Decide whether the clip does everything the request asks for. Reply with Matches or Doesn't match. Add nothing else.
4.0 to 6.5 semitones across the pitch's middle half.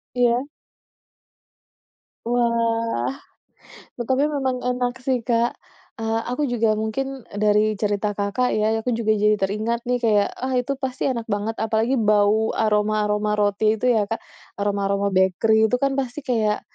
Doesn't match